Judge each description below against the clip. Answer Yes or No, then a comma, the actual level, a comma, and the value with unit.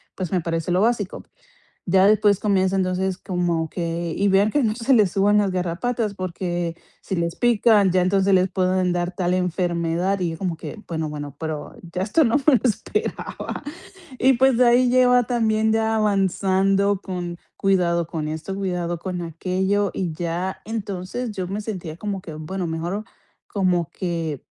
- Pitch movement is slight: No, average, 3.2 semitones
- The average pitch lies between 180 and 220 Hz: Yes, medium, 185 Hz